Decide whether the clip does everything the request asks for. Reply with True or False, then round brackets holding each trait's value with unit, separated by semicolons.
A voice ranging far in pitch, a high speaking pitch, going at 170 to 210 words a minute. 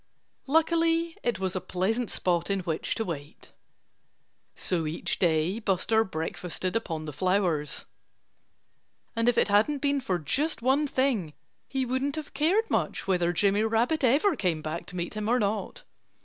False (7.2 semitones; 210 Hz; 160 wpm)